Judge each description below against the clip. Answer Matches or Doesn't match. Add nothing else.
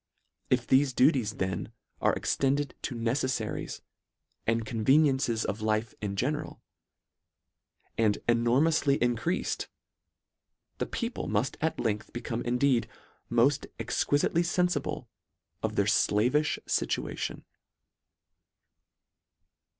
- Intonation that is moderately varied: Matches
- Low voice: Matches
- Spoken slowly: Matches